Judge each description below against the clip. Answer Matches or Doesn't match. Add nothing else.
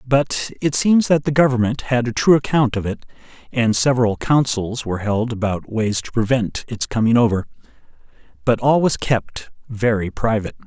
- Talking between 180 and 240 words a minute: Doesn't match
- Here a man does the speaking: Matches